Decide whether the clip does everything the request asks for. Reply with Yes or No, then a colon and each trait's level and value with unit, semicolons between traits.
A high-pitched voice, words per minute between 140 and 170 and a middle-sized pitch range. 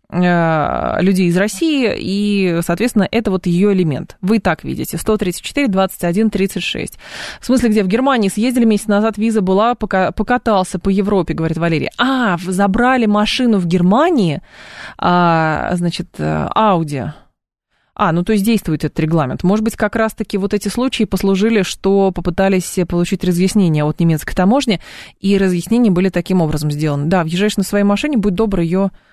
Yes: high, 195 Hz; average, 155 wpm; average, 3.5 semitones